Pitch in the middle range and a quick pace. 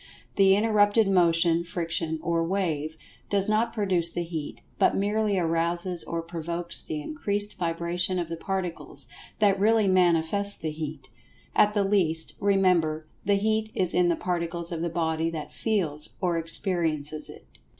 No: medium, 175 Hz; average, 150 wpm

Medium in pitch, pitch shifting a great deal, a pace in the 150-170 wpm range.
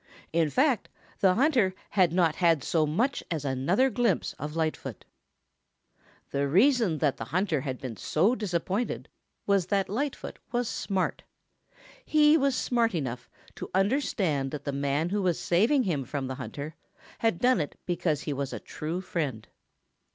Yes: medium, 175 Hz; wide, 7.2 semitones; average, 160 wpm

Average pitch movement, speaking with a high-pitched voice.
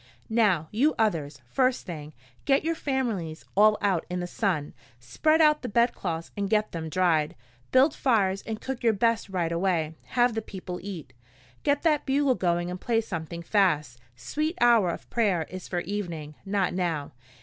No: wide, 5.9 semitones; high, 195 Hz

